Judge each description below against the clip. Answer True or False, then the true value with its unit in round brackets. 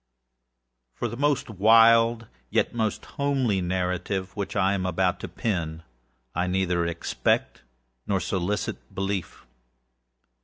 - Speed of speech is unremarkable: False (115 wpm)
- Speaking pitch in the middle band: False (95 Hz)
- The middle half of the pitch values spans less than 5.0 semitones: True (3.8 semitones)